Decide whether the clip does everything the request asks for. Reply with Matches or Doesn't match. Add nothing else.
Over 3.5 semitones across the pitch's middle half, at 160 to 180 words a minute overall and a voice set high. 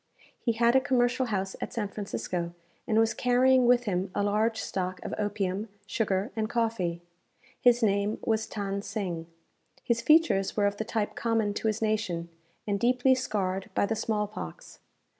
Doesn't match